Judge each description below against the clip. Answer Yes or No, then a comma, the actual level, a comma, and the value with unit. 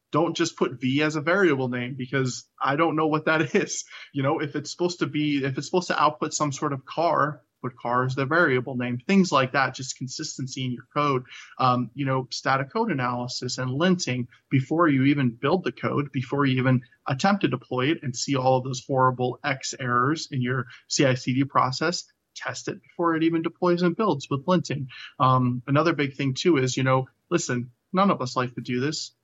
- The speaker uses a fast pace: Yes, fast, 215 wpm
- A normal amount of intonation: Yes, average, 3.7 semitones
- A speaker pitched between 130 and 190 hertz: Yes, low, 135 Hz